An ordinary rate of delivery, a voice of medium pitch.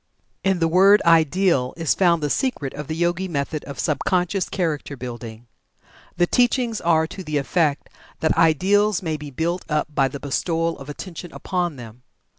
Yes: average, 175 wpm; medium, 165 Hz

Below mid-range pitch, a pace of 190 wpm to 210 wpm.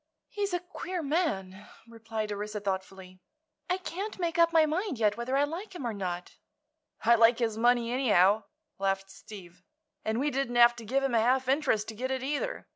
No: high, 235 Hz; average, 195 wpm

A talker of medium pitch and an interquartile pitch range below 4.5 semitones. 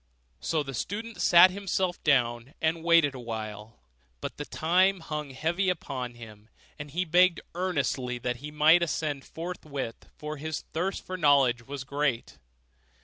No: medium, 150 Hz; average, 5.3 semitones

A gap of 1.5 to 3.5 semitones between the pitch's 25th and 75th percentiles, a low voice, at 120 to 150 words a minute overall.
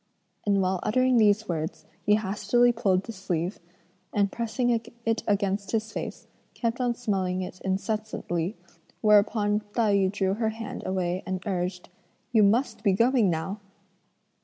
No: average, 3.2 semitones; high, 205 Hz; average, 145 wpm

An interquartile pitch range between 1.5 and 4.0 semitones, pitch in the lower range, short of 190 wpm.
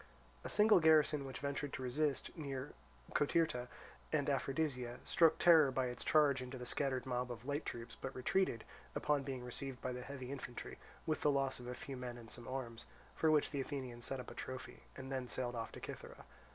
No: narrow, 2.6 semitones; low, 130 Hz; fast, 205 wpm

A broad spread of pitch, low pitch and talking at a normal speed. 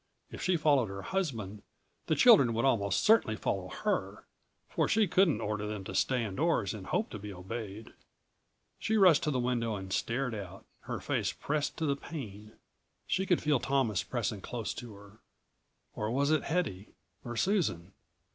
Yes: wide, 6.9 semitones; low, 120 Hz; average, 175 wpm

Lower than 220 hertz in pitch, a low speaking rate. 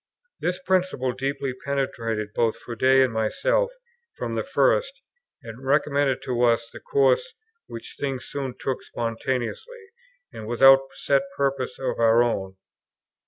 Yes: low, 135 Hz; slow, 130 wpm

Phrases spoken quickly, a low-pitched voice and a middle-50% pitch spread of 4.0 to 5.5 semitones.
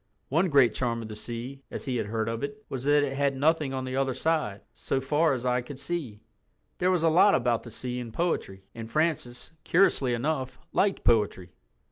Yes: fast, 210 wpm; low, 130 Hz; average, 4.7 semitones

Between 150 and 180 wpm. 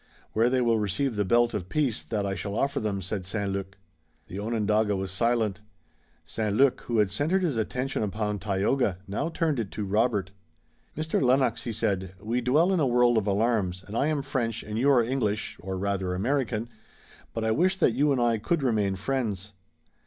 No: average, 195 wpm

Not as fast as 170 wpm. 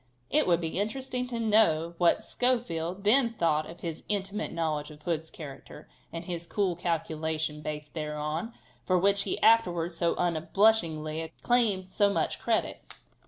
Yes: average, 150 wpm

